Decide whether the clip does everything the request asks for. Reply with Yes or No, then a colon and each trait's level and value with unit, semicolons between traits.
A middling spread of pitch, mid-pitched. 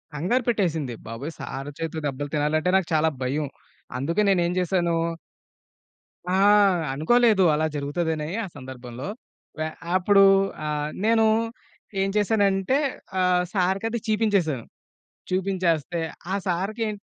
Yes: average, 4.8 semitones; medium, 175 Hz